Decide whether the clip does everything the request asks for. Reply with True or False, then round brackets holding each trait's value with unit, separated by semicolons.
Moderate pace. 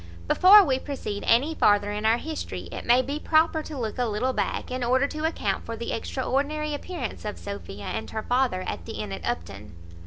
False (210 wpm)